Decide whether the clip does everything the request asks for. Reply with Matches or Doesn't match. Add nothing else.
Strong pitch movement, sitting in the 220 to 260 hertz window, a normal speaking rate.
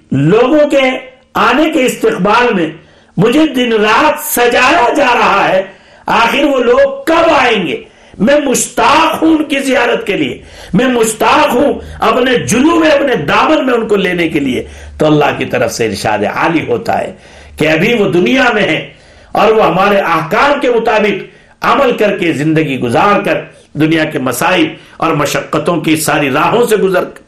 Matches